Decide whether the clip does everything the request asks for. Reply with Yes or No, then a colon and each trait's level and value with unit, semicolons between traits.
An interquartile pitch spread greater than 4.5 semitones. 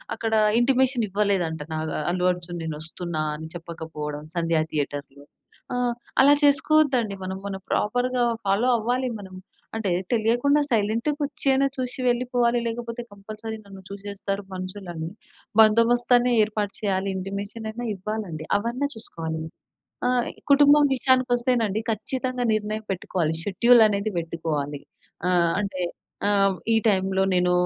Yes: average, 5.2 semitones